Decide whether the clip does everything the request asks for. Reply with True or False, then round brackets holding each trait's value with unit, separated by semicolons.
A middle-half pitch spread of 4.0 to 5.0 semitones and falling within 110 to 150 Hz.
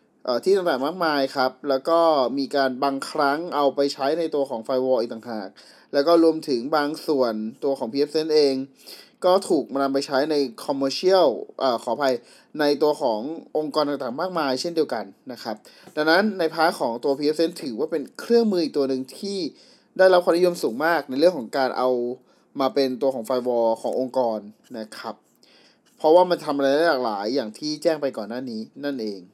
False (3.6 semitones; 140 Hz)